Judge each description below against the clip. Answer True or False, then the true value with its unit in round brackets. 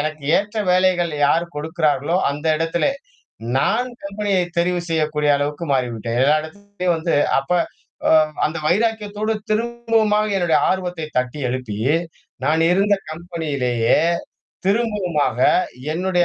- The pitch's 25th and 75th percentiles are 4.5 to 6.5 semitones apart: True (5.0 semitones)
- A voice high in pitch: False (170 Hz)